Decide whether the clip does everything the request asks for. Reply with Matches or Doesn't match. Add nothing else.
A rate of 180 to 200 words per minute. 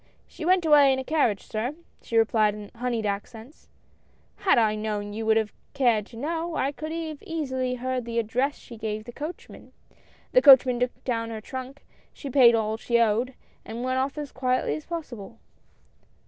Matches